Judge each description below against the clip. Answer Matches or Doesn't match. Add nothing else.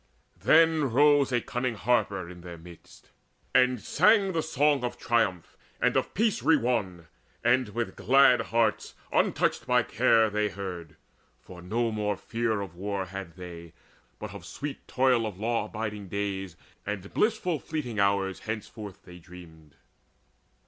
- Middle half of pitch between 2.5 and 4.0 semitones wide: Doesn't match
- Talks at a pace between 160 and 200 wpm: Doesn't match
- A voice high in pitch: Doesn't match